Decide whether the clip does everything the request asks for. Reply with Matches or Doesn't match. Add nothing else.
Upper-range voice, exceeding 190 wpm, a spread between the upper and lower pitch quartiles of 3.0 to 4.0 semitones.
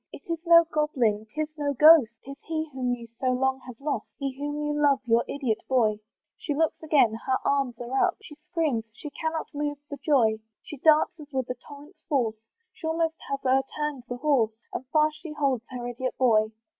Matches